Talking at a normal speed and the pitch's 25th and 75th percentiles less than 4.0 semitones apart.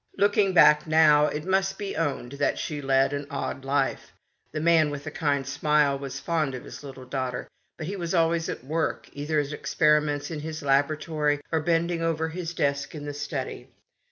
Yes: average, 190 wpm; narrow, 2.5 semitones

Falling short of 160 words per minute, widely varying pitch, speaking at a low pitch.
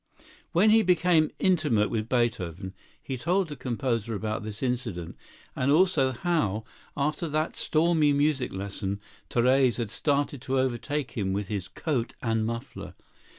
Yes: average, 145 wpm; wide, 5.8 semitones; low, 130 Hz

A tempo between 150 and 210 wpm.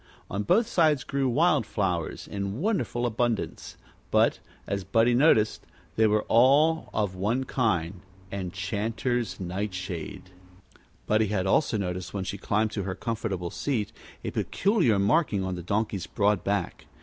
No: average, 140 wpm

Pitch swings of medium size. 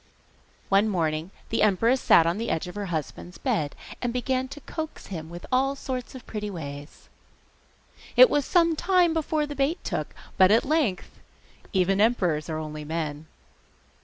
No: wide, 8.5 semitones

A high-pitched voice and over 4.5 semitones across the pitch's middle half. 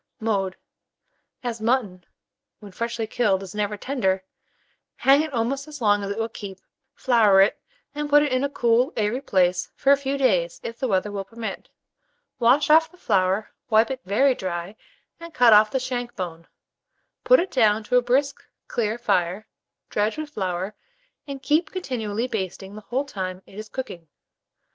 Yes: high, 225 Hz; average, 5.1 semitones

